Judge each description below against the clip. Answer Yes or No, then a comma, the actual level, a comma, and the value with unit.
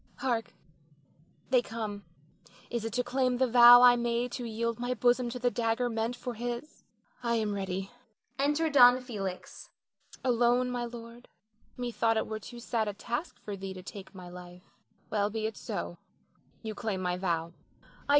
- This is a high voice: Yes, high, 235 Hz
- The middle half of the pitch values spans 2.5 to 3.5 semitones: Yes, average, 2.9 semitones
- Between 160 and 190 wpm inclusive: Yes, average, 170 wpm